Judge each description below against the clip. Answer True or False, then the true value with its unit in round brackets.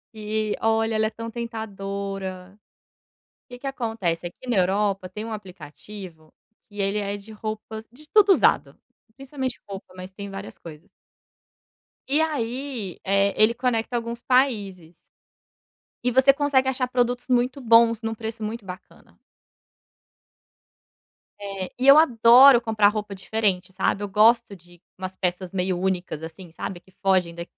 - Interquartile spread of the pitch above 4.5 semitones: False (3.9 semitones)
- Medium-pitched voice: False (215 Hz)